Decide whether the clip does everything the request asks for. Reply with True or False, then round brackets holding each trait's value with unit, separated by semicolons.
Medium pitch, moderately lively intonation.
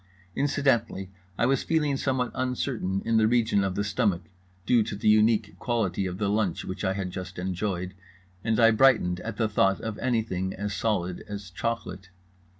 False (105 Hz; 3.5 semitones)